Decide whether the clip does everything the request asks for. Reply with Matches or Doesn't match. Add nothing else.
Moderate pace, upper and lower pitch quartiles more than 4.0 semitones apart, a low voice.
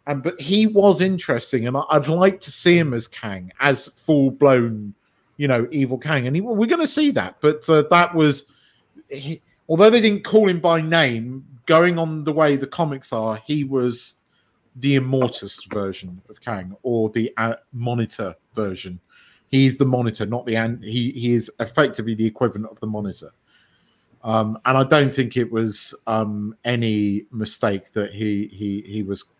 Matches